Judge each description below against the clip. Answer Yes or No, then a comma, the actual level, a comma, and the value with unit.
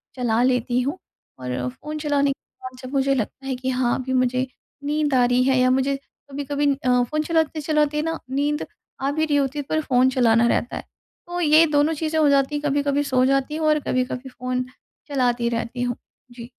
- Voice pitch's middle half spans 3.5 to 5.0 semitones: No, average, 2.8 semitones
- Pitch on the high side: Yes, very high, 270 Hz